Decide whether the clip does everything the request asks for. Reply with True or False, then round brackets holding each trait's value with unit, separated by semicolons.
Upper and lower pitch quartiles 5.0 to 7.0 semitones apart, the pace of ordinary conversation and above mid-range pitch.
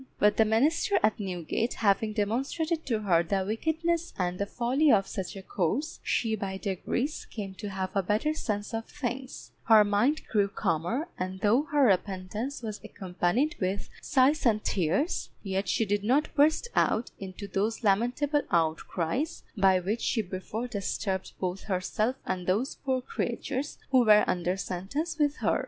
True (5.4 semitones; 165 wpm; 215 Hz)